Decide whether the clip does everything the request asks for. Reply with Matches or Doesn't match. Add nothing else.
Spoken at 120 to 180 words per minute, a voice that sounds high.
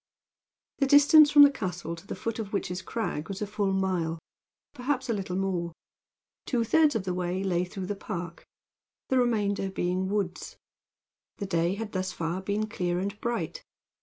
Matches